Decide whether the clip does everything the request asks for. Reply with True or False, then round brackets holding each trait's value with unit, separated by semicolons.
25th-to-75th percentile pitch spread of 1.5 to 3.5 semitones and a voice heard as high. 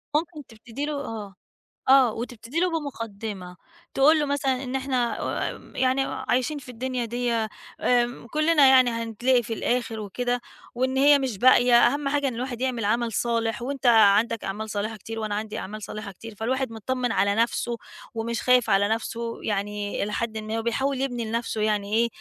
True (3.0 semitones; 235 Hz)